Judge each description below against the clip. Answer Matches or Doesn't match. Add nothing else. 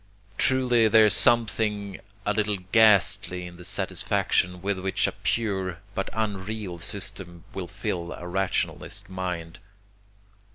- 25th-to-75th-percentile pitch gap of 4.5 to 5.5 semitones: Doesn't match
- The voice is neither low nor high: Doesn't match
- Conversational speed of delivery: Doesn't match